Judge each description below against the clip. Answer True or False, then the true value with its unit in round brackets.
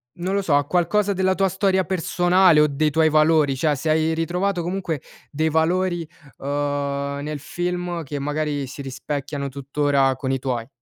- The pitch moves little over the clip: False (3.8 semitones)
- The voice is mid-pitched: True (155 Hz)